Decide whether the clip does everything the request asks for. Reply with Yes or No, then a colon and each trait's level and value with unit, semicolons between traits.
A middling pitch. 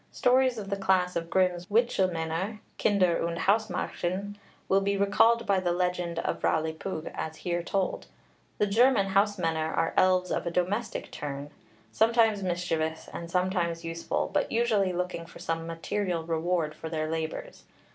Yes: medium, 180 Hz